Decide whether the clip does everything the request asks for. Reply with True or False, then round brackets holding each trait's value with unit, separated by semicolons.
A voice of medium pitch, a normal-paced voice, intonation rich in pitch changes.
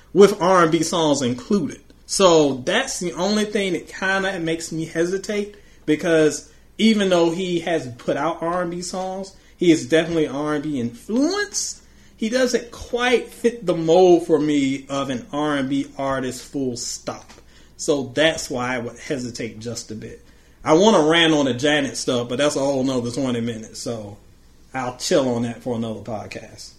True (155 Hz; 170 wpm; 6.4 semitones)